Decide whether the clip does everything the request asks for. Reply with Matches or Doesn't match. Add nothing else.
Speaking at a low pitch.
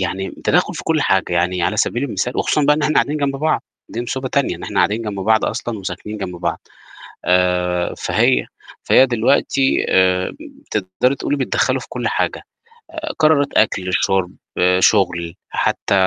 Matches